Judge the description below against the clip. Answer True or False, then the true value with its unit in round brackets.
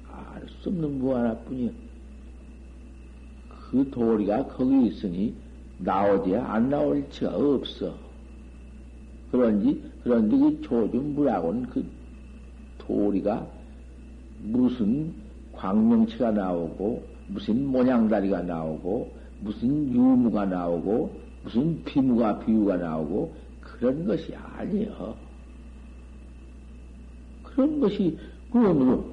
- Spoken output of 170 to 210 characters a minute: True (200 characters per minute)